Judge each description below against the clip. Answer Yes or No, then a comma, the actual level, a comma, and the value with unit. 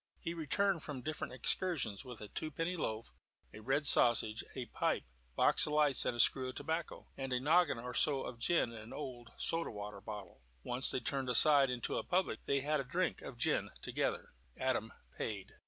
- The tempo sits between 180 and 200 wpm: Yes, average, 190 wpm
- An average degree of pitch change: Yes, average, 4.6 semitones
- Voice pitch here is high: No, low, 130 Hz